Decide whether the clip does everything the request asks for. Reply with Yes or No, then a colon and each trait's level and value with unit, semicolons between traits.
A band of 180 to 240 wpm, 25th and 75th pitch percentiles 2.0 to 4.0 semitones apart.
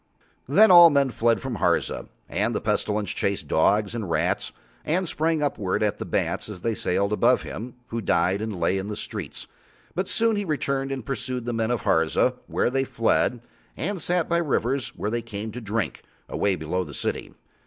No: average, 195 wpm; average, 5.3 semitones